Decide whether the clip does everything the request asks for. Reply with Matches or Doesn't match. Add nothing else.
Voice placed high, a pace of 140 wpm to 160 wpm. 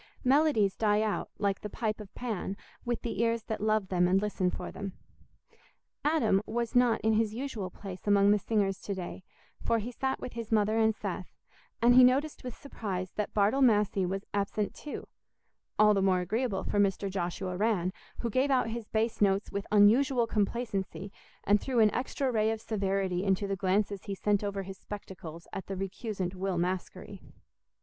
Doesn't match